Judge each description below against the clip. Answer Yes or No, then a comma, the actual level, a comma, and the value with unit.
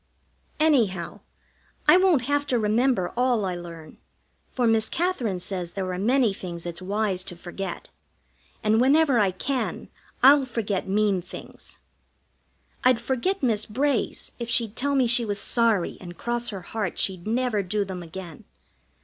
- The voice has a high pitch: Yes, high, 215 Hz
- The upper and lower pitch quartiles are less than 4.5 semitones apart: No, average, 5.2 semitones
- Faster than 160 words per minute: No, average, 155 wpm